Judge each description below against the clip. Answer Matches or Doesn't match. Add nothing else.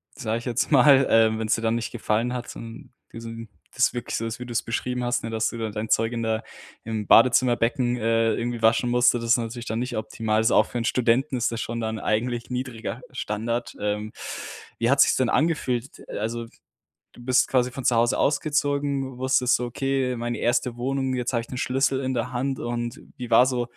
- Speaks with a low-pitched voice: Matches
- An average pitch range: Doesn't match